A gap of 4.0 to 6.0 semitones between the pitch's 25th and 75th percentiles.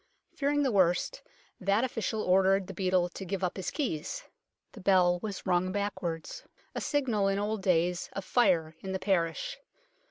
No: average, 3.0 semitones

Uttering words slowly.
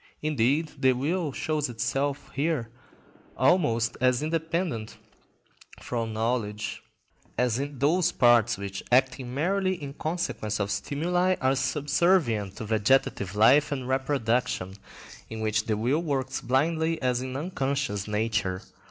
Yes: slow, 125 wpm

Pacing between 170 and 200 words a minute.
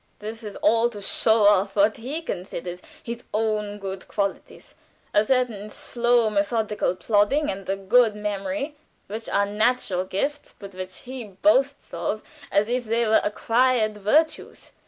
No: average, 150 wpm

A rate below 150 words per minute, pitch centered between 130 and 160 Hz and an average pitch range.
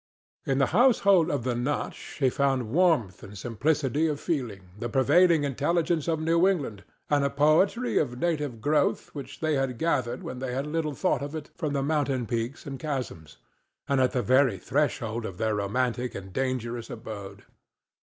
No: average, 170 wpm; low, 135 Hz; average, 4.4 semitones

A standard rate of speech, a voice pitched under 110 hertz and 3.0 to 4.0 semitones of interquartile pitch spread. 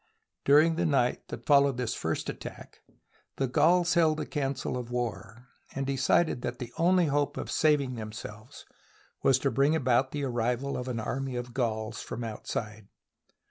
No: average, 165 wpm; low, 130 Hz; average, 3.3 semitones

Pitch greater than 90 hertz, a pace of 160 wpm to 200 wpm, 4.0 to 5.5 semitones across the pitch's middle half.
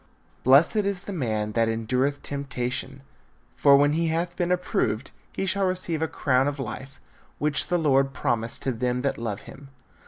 Yes: medium, 140 Hz; average, 175 wpm; average, 4.7 semitones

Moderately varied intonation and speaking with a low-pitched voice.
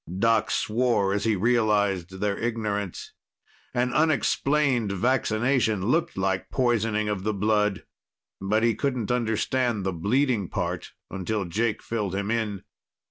Yes: average, 3.3 semitones; low, 110 Hz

